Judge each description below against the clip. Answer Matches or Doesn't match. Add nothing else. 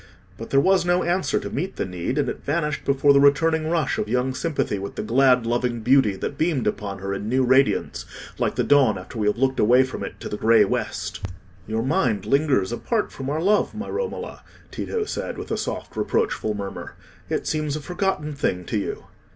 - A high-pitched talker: Doesn't match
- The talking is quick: Matches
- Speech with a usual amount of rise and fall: Doesn't match